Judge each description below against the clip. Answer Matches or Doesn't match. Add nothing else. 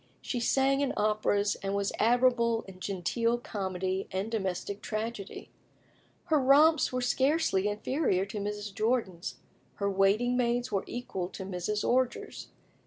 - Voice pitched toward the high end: Matches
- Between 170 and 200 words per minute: Doesn't match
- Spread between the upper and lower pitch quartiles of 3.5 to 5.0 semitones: Matches